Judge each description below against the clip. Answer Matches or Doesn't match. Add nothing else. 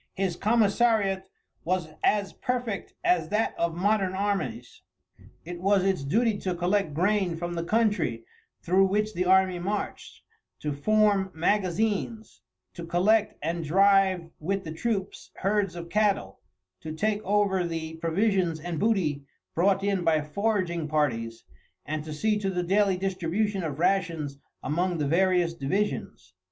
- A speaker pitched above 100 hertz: Matches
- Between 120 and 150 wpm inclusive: Matches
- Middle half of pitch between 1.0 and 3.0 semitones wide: Doesn't match